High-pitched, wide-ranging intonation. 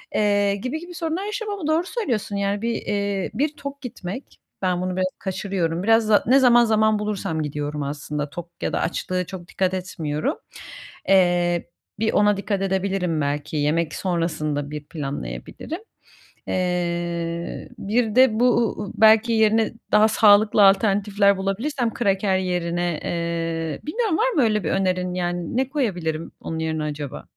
No: high, 195 Hz; average, 4.6 semitones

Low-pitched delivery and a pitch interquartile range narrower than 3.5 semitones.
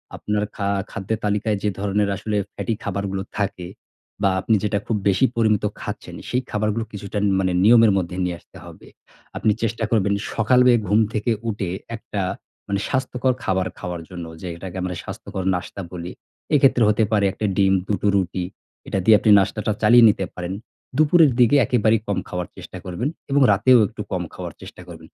Yes: low, 105 Hz; average, 2.9 semitones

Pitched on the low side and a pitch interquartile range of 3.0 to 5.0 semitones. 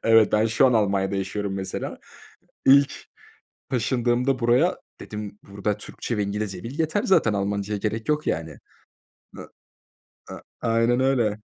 Yes: low, 110 Hz; average, 3.3 semitones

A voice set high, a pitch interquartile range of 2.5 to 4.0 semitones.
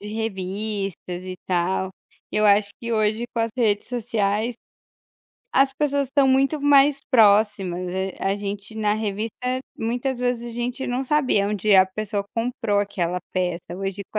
Yes: high, 215 Hz; average, 3.7 semitones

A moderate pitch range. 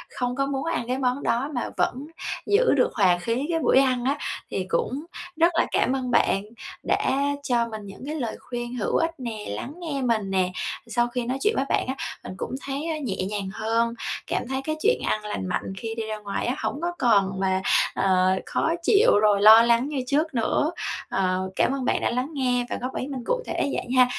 Yes: average, 4.4 semitones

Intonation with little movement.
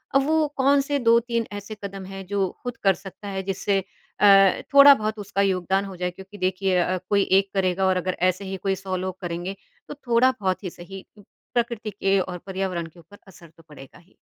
Yes: narrow, 2.2 semitones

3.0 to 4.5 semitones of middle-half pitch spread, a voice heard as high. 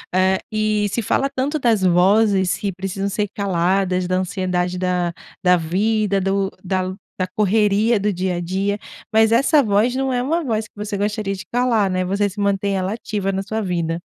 No: narrow, 2.6 semitones; high, 200 Hz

